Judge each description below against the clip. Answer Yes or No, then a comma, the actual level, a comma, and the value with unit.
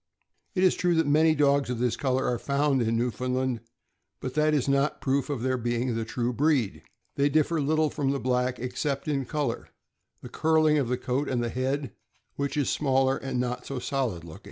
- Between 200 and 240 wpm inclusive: Yes, fast, 205 wpm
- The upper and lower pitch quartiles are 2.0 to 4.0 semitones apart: Yes, average, 2.7 semitones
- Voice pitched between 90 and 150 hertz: Yes, low, 135 Hz